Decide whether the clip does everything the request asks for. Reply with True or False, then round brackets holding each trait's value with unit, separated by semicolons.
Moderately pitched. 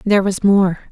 False (195 Hz)